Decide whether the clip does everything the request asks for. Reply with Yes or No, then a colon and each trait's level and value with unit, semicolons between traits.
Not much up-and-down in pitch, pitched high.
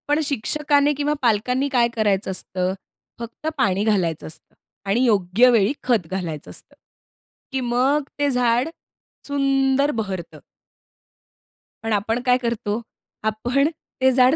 No: average, 4.7 semitones; high, 240 Hz